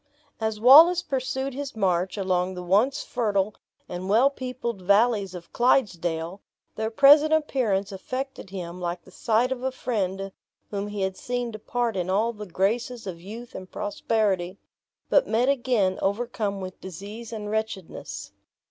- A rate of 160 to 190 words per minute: No, average, 150 wpm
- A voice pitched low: No, high, 210 Hz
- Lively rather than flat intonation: No, average, 4.5 semitones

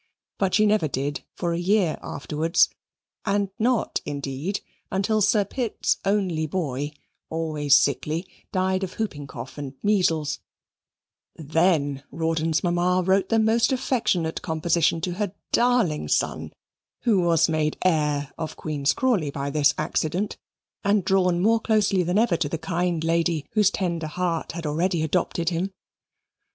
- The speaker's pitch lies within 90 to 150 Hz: No, medium, 170 Hz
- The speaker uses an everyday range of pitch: Yes, average, 4.1 semitones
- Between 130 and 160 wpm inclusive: Yes, average, 140 wpm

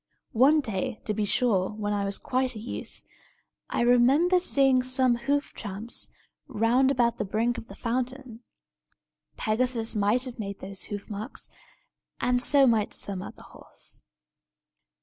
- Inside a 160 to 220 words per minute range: No, average, 150 wpm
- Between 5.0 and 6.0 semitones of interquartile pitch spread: No, average, 3.4 semitones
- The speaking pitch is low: No, high, 235 Hz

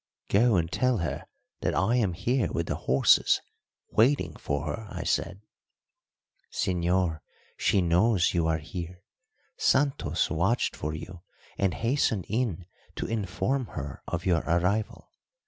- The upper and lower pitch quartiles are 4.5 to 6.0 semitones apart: Yes, average, 5.0 semitones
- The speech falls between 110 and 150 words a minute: Yes, slow, 135 wpm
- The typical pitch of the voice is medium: No, very low, 90 Hz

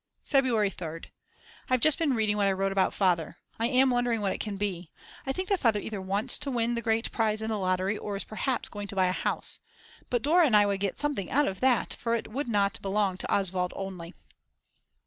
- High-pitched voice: Yes, high, 210 Hz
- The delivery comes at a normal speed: No, fast, 230 wpm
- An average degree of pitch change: Yes, average, 3.9 semitones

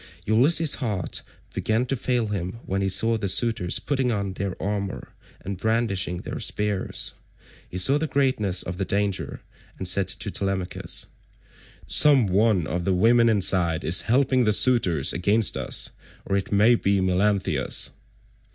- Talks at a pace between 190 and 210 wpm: No, average, 150 wpm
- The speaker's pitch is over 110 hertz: No, low, 100 Hz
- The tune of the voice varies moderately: Yes, average, 3.8 semitones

